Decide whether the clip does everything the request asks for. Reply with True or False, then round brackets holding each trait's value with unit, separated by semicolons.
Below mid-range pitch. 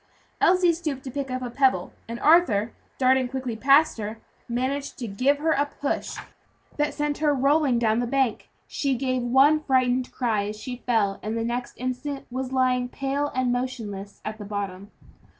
False (255 Hz)